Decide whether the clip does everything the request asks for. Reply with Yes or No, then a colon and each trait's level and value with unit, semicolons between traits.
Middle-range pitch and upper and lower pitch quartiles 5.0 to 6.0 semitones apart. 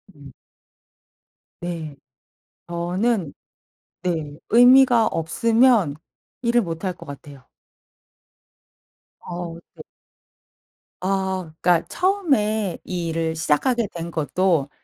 Yes: medium, 175 Hz; wide, 5.5 semitones